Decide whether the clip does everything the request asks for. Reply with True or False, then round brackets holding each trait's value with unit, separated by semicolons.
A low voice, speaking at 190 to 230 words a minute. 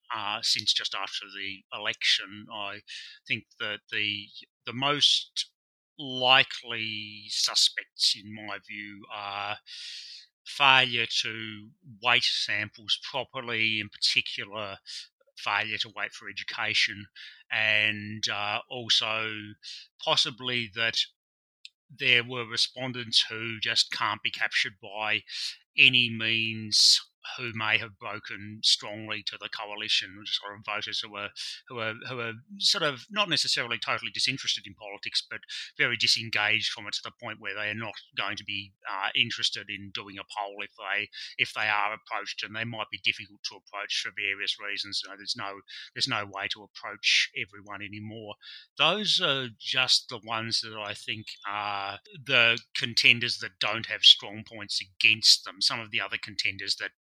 False (110 Hz; 150 wpm)